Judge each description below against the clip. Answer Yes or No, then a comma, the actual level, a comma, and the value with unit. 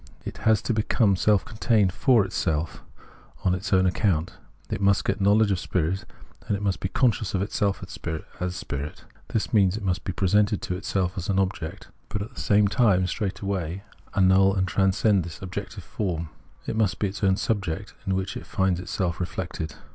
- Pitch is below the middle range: Yes, very low, 95 Hz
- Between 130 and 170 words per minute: No, average, 185 wpm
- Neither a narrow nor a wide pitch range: No, narrow, 2.1 semitones